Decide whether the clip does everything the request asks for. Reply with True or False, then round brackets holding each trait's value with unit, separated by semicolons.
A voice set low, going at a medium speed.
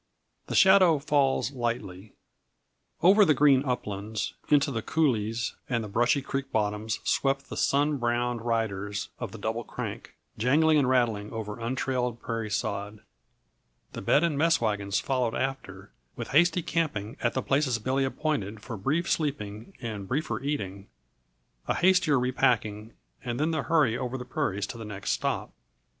True (120 Hz; 155 wpm)